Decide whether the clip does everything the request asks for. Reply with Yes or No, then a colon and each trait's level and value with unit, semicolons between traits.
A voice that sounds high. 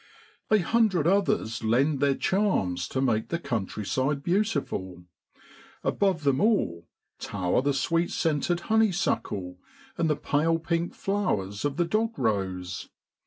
No: medium, 145 Hz